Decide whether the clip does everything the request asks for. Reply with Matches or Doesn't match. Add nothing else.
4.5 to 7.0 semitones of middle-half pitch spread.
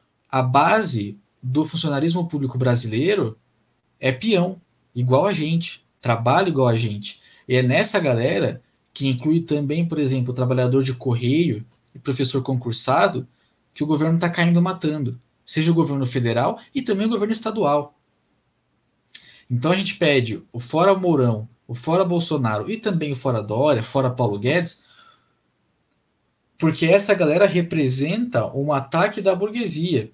Matches